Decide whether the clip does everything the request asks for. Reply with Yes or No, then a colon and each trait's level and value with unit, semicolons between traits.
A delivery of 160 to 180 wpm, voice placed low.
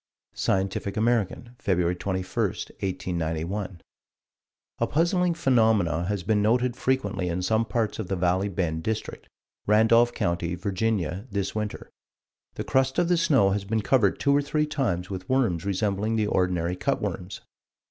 No: average, 145 wpm; low, 100 Hz